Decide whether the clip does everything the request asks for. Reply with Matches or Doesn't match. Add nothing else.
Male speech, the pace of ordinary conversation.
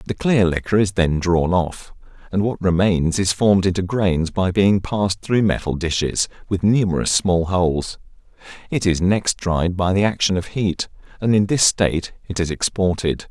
Matches